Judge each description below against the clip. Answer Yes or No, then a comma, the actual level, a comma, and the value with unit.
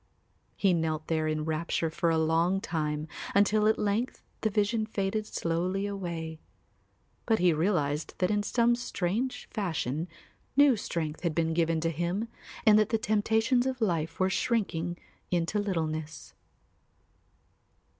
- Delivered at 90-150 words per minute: Yes, average, 145 wpm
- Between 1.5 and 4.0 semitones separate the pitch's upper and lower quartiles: No, average, 4.8 semitones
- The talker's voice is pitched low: No, medium, 180 Hz